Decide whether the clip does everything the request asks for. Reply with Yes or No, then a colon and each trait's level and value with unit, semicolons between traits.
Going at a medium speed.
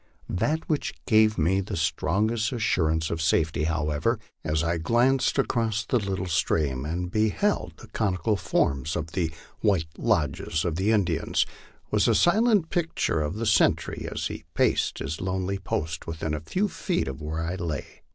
Yes: average, 160 wpm